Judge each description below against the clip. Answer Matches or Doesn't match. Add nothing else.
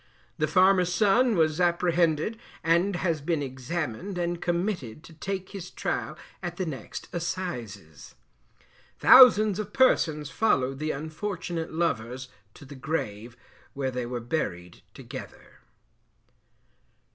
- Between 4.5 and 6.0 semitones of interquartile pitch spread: Matches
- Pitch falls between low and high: Matches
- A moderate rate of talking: Doesn't match